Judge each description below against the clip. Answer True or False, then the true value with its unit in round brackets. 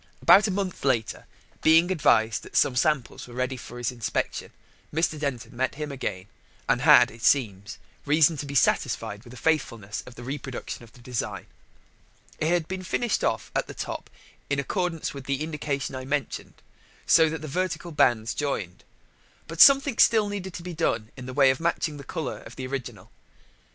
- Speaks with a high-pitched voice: False (140 Hz)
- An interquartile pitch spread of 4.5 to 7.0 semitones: True (4.9 semitones)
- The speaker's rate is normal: True (185 wpm)